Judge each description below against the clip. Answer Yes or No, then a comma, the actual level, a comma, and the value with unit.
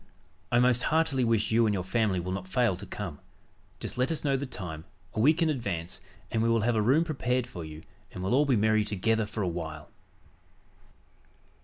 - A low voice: Yes, low, 110 Hz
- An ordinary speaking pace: No, fast, 210 wpm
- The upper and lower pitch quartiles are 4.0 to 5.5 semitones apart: Yes, average, 5.2 semitones